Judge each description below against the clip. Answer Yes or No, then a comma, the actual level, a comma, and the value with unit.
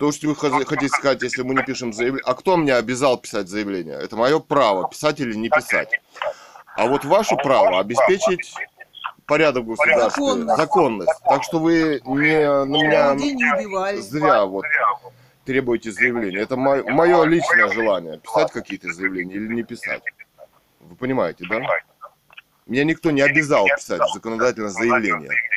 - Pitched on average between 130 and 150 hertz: Yes, medium, 140 Hz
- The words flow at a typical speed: Yes, average, 145 wpm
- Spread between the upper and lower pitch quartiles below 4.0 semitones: No, average, 5.3 semitones